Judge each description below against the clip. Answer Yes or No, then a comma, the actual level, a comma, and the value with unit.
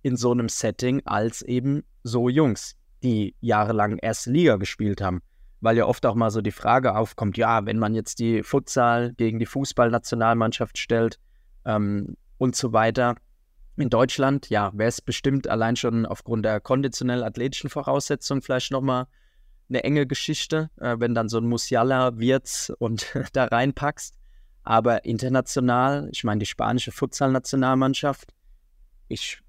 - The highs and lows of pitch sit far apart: No, average, 2.9 semitones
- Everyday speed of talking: Yes, average, 150 wpm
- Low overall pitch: Yes, low, 120 Hz